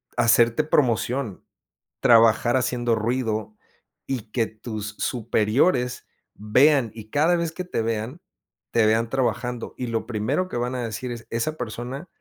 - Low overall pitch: Yes, low, 120 Hz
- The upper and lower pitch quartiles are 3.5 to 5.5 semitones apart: No, average, 2.8 semitones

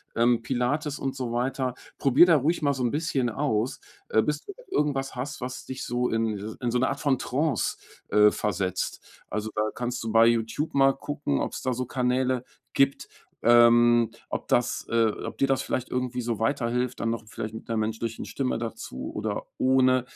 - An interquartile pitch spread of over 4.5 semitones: No, average, 2.8 semitones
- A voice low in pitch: Yes, low, 125 Hz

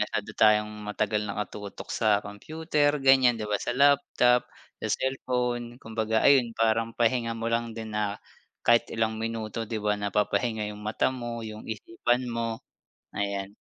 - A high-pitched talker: No, low, 115 Hz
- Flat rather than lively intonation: Yes, narrow, 2.2 semitones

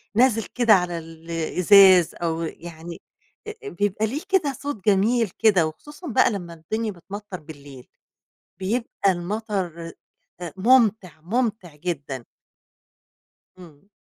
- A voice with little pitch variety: No, average, 5.0 semitones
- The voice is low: No, high, 190 Hz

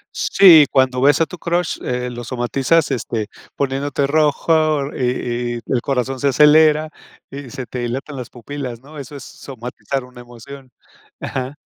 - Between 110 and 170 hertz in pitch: Yes, low, 135 Hz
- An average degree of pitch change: Yes, average, 3.0 semitones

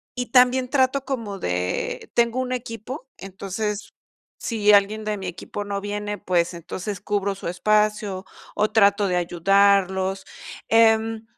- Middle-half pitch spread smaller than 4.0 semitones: Yes, average, 2.8 semitones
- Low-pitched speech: No, high, 205 Hz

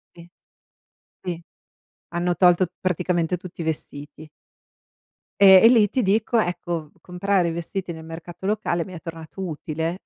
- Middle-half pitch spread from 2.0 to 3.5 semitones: Yes, narrow, 2.5 semitones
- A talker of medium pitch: Yes, medium, 175 Hz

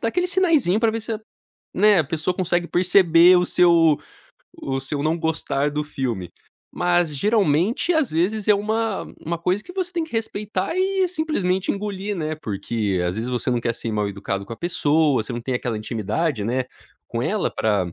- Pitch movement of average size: No, wide, 8.4 semitones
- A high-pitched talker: No, medium, 170 Hz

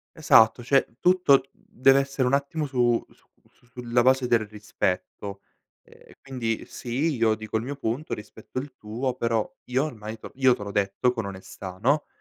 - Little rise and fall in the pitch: No, average, 3.7 semitones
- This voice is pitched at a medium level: No, low, 120 Hz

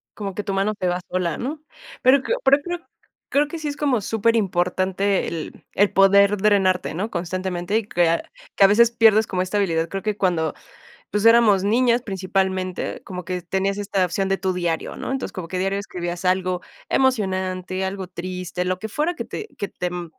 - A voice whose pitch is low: No, high, 195 Hz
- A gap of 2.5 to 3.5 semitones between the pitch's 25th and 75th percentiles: Yes, average, 2.8 semitones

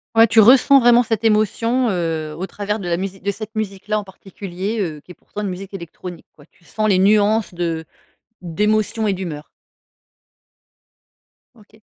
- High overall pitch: Yes, high, 200 Hz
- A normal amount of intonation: Yes, average, 3.2 semitones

